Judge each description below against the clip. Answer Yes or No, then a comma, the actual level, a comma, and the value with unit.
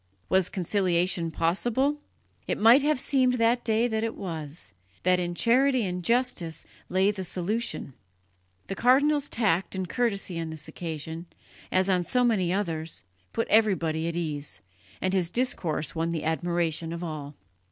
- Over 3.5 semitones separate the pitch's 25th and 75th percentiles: Yes, wide, 5.5 semitones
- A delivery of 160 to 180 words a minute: No, average, 150 wpm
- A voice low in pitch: No, medium, 185 Hz